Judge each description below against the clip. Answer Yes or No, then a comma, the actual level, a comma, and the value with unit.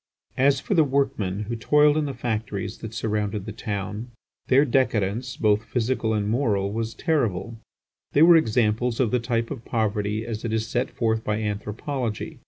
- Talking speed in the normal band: Yes, average, 175 wpm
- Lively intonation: No, average, 3.3 semitones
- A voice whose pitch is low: Yes, low, 115 Hz